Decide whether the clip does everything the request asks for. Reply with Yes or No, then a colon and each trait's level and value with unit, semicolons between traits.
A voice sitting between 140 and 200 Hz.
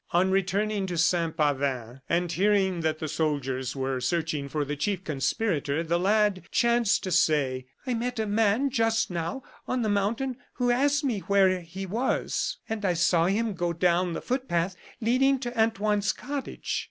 Yes: high, 190 Hz